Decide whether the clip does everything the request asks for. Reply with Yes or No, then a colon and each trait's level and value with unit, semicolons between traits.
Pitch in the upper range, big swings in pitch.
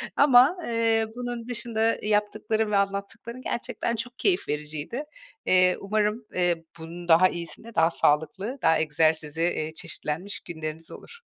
Yes: high, 200 Hz; wide, 6.1 semitones